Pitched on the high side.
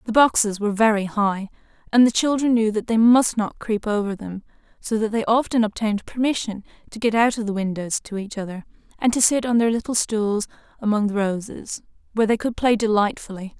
Yes: high, 220 Hz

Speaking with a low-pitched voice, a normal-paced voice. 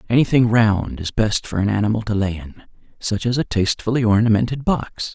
Yes: low, 110 Hz; average, 185 wpm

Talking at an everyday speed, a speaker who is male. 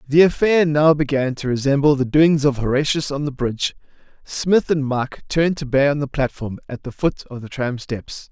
No: fast, 215 wpm; male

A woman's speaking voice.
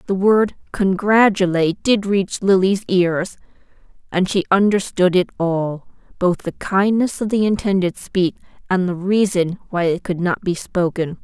Yes: female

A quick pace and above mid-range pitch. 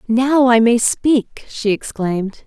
No: average, 145 wpm; high, 235 Hz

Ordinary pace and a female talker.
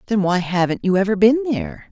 No: fast, 220 wpm; female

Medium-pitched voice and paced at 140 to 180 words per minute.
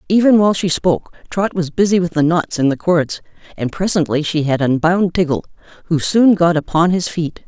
No: medium, 170 Hz; average, 200 wpm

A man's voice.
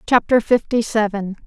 No: female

